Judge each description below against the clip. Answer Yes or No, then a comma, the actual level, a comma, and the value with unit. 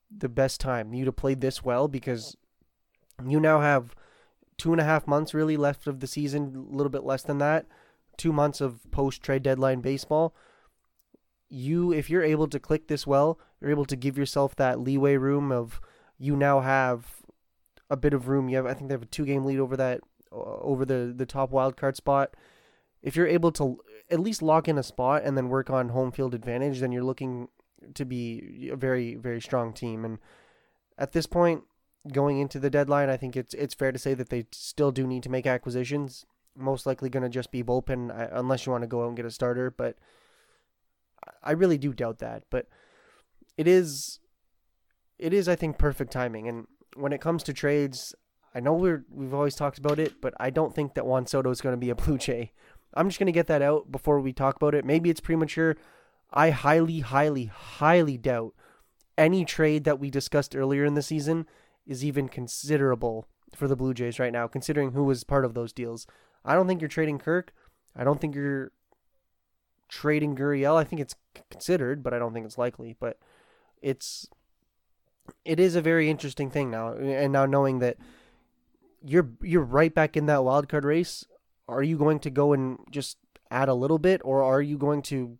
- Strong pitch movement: No, narrow, 2.6 semitones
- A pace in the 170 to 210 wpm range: Yes, fast, 205 wpm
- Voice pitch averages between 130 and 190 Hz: Yes, medium, 140 Hz